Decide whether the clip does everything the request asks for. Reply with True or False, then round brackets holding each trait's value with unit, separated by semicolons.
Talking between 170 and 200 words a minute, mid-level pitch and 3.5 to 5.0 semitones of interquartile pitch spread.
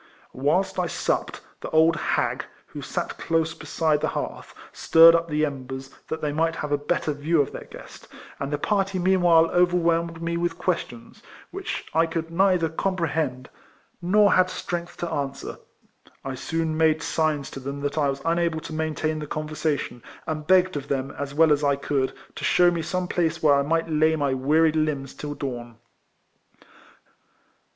False (175 wpm; 160 Hz; 2.8 semitones)